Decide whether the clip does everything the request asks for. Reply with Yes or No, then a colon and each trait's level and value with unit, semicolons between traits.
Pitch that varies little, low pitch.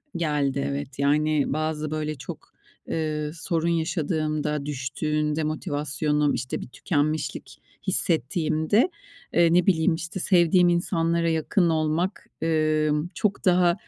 No: narrow, 2.0 semitones; medium, 155 Hz